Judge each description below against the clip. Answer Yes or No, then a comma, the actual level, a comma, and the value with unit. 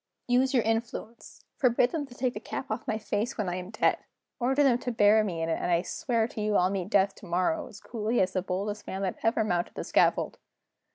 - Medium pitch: No, high, 215 Hz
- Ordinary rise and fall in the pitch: Yes, average, 4.3 semitones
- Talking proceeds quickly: Yes, fast, 235 wpm